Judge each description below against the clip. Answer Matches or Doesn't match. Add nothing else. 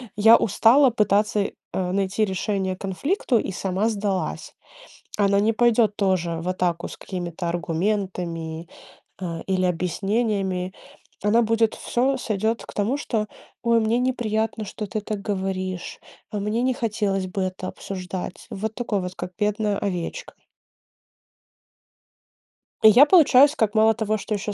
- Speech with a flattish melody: Doesn't match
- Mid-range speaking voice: Doesn't match